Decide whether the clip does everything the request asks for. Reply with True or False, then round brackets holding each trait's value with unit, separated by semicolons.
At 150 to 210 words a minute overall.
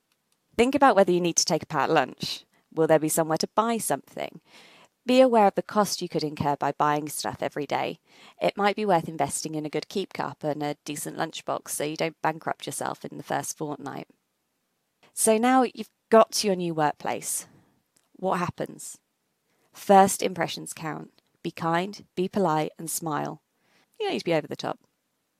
True (190 wpm)